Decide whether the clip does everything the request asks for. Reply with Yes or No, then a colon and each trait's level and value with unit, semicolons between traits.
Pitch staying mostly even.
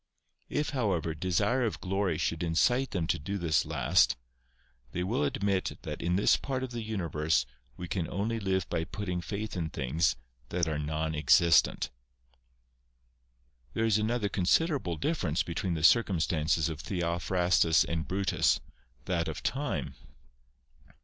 No: average, 4.2 semitones